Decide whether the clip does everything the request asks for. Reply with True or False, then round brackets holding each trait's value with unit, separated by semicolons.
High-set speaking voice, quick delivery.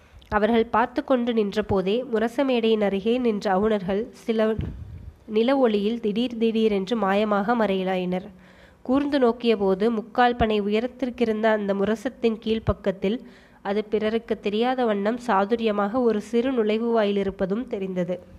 False (220 Hz; 110 wpm)